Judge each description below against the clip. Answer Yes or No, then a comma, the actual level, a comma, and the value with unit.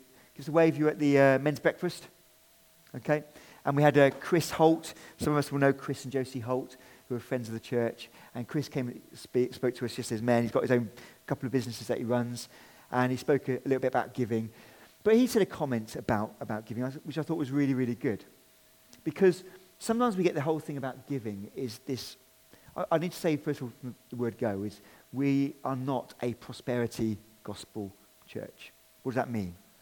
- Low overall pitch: Yes, low, 130 Hz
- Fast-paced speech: Yes, fast, 225 wpm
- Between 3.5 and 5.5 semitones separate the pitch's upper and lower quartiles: Yes, average, 3.8 semitones